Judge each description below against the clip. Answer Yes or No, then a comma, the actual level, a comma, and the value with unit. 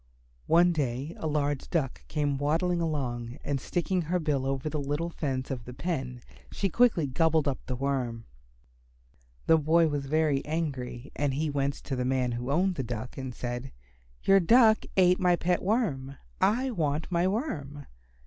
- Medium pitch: Yes, medium, 145 Hz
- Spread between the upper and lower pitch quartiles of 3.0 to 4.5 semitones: Yes, average, 4.2 semitones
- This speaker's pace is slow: No, average, 175 wpm